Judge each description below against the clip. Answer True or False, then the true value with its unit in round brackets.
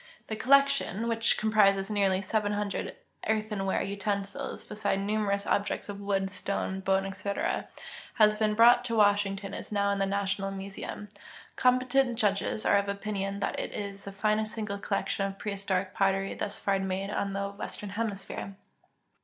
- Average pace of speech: True (155 wpm)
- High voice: True (200 Hz)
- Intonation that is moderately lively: False (1.5 semitones)